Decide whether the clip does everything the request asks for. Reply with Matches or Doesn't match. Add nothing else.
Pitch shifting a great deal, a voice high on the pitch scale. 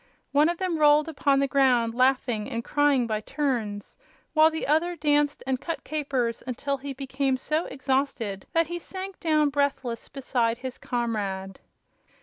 Doesn't match